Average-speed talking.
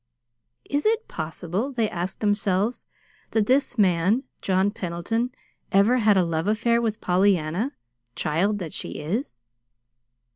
No: slow, 125 wpm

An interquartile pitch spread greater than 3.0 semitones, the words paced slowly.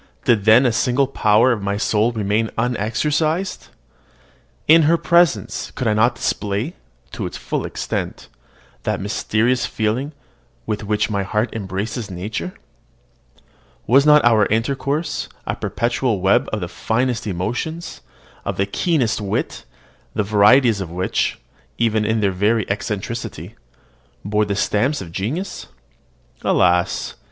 Yes: average, 3.8 semitones; slow, 130 wpm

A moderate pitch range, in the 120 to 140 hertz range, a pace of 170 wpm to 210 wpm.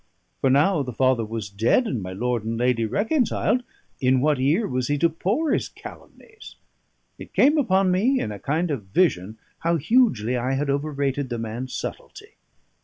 No: wide, 7.5 semitones; low, 135 Hz; average, 180 wpm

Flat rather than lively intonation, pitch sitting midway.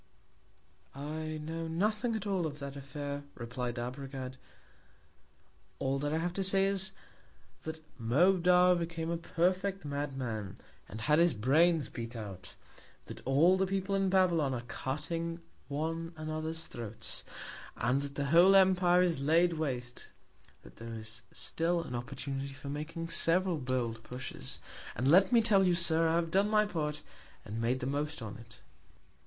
No: average, 5.0 semitones; medium, 155 Hz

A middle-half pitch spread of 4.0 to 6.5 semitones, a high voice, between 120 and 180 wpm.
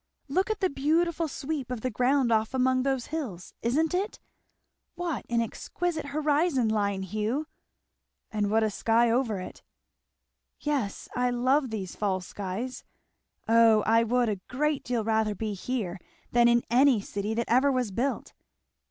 Yes: average, 4.4 semitones; high, 245 Hz; average, 155 wpm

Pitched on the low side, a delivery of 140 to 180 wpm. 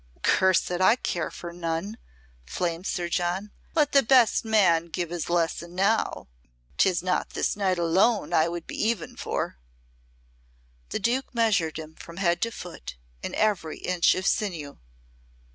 No: medium, 180 Hz; average, 155 wpm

